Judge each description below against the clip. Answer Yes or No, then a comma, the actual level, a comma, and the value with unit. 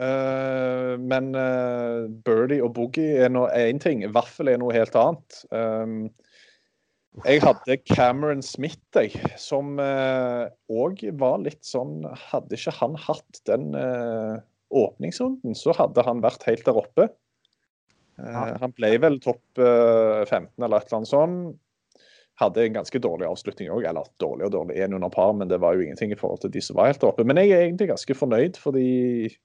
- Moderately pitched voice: No, low, 125 Hz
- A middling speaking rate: Yes, average, 175 wpm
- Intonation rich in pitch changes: No, average, 3.3 semitones